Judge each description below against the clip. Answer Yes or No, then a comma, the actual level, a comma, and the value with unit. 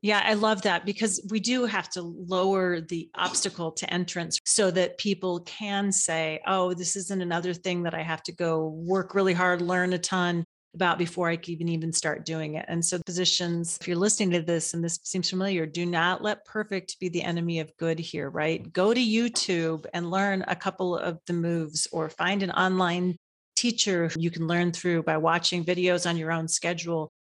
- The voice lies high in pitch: No, medium, 175 Hz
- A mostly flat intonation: Yes, narrow, 2.1 semitones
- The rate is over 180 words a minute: Yes, fast, 205 wpm